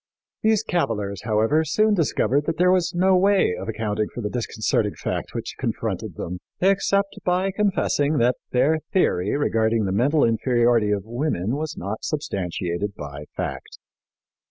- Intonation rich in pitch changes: Yes, wide, 8.8 semitones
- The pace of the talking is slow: No, average, 155 wpm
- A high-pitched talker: No, low, 120 Hz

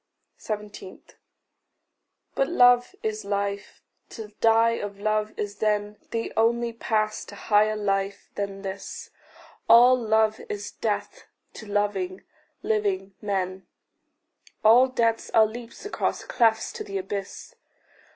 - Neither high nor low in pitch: No, high, 215 Hz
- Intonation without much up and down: Yes, narrow, 2.1 semitones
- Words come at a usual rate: No, slow, 120 wpm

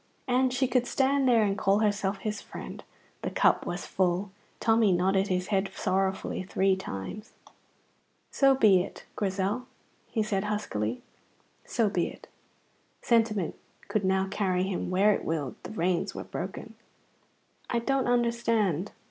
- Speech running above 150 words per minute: No, average, 145 wpm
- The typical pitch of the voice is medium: No, high, 200 Hz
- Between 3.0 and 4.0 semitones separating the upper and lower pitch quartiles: Yes, average, 3.4 semitones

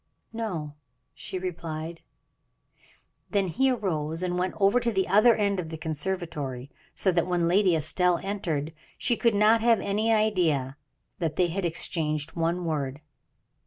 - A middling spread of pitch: Yes, average, 4.1 semitones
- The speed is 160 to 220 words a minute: No, average, 150 wpm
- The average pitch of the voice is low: No, medium, 180 Hz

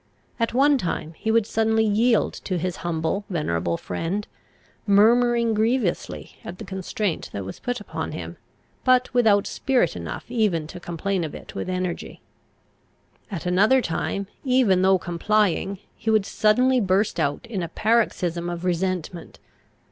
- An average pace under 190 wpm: Yes, average, 150 wpm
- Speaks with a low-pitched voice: No, high, 200 Hz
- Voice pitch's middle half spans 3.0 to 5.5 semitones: Yes, average, 4.5 semitones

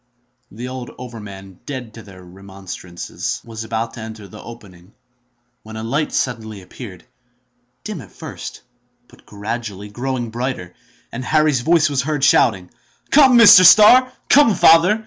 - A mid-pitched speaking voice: No, low, 115 Hz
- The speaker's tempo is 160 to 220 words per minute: No, average, 140 wpm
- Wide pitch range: Yes, wide, 6.3 semitones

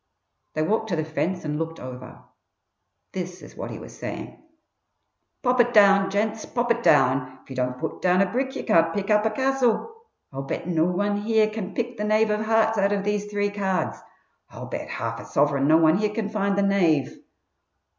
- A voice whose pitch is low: No, high, 200 Hz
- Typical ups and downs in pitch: Yes, average, 5.0 semitones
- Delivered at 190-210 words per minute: Yes, fast, 205 wpm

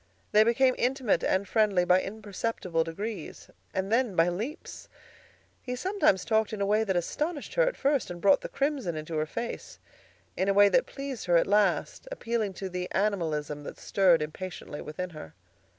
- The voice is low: No, high, 200 Hz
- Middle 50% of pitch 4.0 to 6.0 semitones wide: Yes, average, 5.0 semitones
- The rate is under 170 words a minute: No, average, 180 wpm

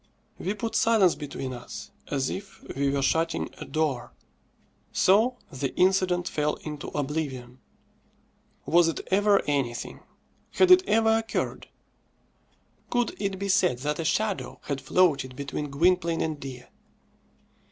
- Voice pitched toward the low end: No, medium, 165 Hz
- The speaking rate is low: Yes, slow, 130 wpm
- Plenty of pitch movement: Yes, wide, 5.8 semitones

